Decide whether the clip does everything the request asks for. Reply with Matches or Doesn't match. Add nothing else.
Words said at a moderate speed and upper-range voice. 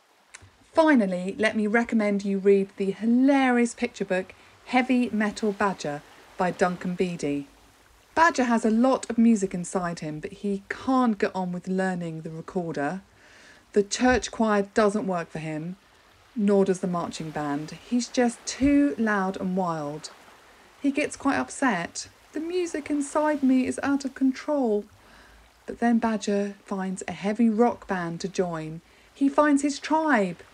Matches